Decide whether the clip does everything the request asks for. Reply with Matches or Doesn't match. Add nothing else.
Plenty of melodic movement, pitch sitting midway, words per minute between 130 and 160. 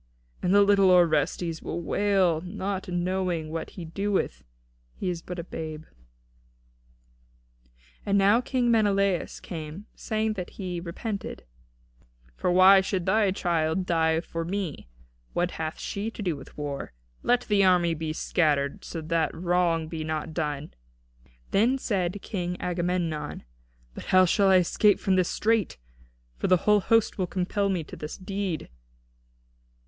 Doesn't match